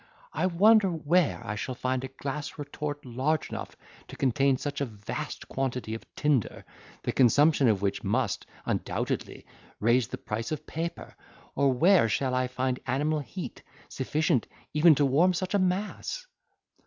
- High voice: No, medium, 140 Hz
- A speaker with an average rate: Yes, average, 155 wpm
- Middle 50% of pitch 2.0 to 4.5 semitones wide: Yes, average, 3.9 semitones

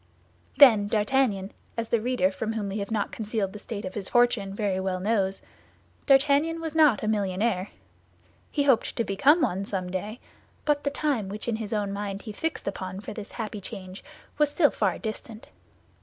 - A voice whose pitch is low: No, high, 215 Hz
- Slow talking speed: No, average, 180 wpm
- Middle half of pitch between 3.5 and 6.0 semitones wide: Yes, average, 3.9 semitones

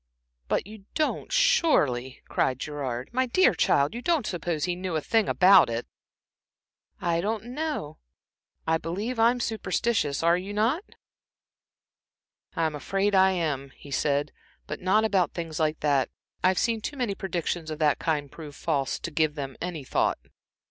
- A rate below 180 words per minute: Yes, average, 160 wpm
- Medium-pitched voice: Yes, medium, 175 Hz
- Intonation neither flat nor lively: No, wide, 6.6 semitones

